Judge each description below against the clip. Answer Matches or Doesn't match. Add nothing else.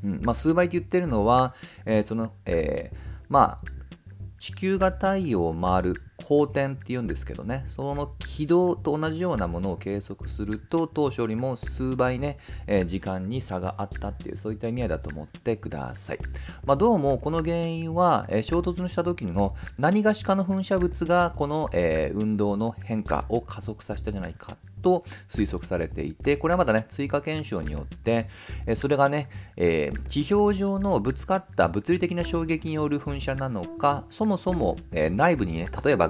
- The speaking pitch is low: Matches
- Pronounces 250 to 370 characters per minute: Matches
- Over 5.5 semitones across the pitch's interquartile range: Matches